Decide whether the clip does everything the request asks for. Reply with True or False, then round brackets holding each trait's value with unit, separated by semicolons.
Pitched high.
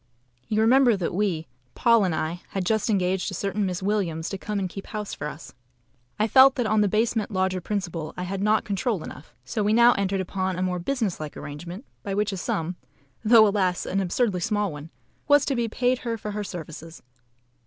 True (195 Hz)